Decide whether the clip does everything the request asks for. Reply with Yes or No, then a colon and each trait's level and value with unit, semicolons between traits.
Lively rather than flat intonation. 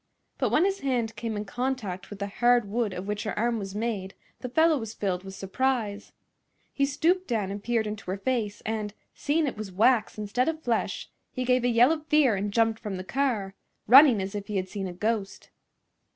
No: average, 4.0 semitones